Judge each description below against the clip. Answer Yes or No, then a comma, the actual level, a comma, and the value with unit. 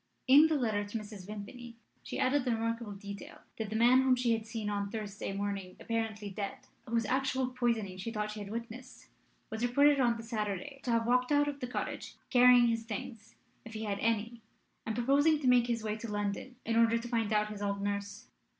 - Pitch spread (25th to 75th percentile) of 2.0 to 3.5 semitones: Yes, average, 3.0 semitones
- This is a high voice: Yes, high, 230 Hz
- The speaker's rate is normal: No, fast, 215 wpm